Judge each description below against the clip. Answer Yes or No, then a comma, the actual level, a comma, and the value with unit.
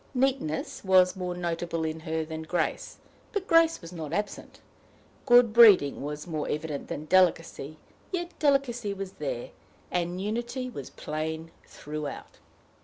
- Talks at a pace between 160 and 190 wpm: No, slow, 135 wpm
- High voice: No, medium, 180 Hz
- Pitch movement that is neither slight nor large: No, wide, 7.1 semitones